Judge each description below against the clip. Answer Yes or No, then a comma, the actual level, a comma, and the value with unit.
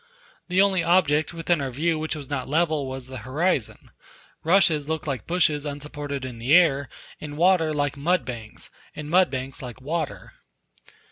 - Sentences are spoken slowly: No, average, 165 wpm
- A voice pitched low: No, medium, 150 Hz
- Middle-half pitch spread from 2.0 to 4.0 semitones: Yes, average, 3.7 semitones